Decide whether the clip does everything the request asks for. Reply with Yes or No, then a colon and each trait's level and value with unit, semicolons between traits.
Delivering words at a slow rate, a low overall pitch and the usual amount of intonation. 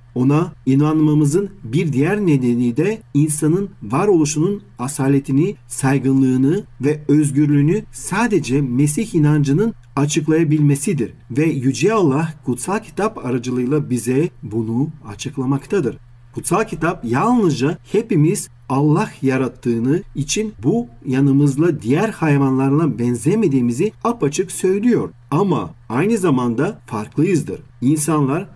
No: slow, 90 wpm; medium, 145 Hz; average, 4.2 semitones